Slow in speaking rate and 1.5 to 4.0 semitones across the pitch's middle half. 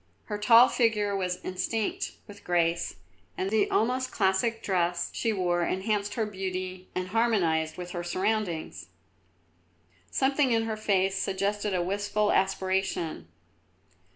Yes: slow, 125 wpm; average, 2.9 semitones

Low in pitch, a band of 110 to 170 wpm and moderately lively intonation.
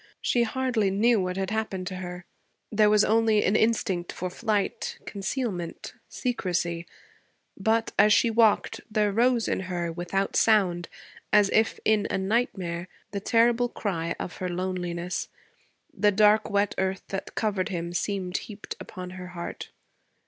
No: high, 200 Hz; average, 150 wpm; average, 3.2 semitones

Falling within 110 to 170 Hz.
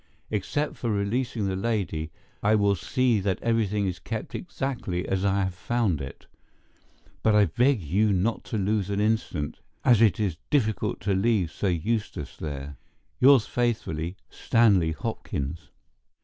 No: low, 100 Hz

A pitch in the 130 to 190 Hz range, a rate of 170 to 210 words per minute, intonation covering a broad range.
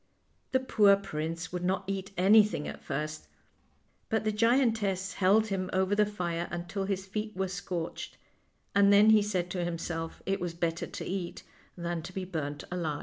No: medium, 185 Hz; average, 175 wpm; average, 2.9 semitones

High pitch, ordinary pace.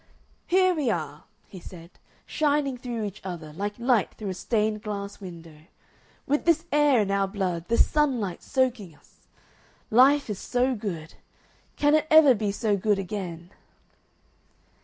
Yes: high, 210 Hz; average, 150 wpm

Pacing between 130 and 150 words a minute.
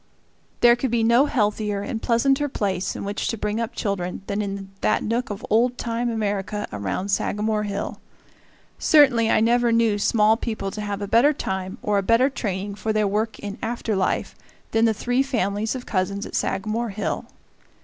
No: average, 185 wpm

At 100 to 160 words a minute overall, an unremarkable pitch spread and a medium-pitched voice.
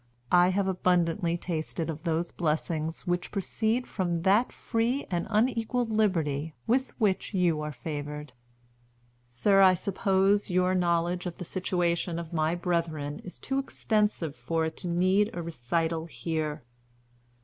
Yes: average, 140 wpm; average, 3.3 semitones; medium, 175 Hz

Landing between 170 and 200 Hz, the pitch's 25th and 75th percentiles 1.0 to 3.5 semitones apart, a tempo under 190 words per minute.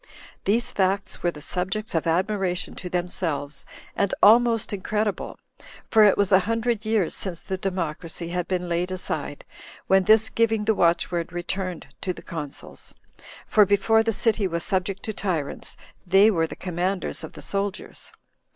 Yes: high, 190 Hz; average, 3.2 semitones; average, 160 wpm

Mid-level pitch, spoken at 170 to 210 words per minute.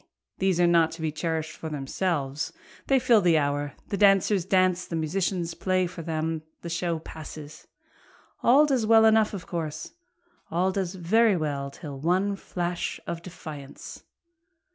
No: medium, 170 Hz; average, 155 wpm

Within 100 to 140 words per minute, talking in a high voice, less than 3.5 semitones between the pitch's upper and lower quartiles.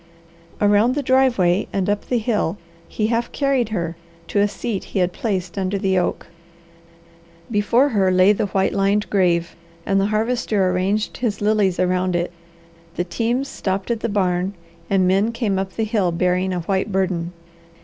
No: average, 170 wpm; high, 195 Hz; average, 2.9 semitones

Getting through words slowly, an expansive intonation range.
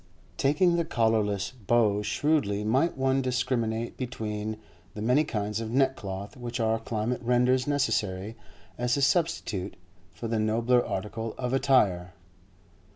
No: slow, 130 wpm; average, 3.6 semitones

